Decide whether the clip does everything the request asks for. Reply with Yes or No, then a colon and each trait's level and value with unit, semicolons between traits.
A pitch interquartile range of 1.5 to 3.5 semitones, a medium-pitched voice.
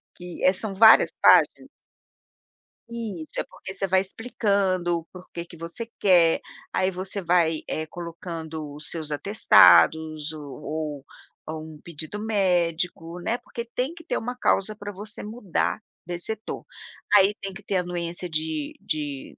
No: average, 4.0 semitones; medium, 180 Hz